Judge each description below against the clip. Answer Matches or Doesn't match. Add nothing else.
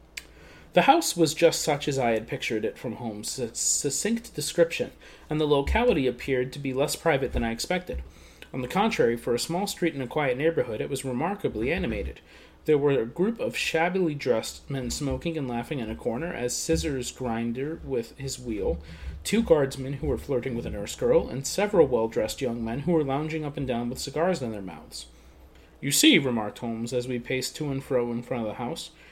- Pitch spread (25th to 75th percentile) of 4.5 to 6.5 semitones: Matches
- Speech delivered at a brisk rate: Matches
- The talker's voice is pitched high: Doesn't match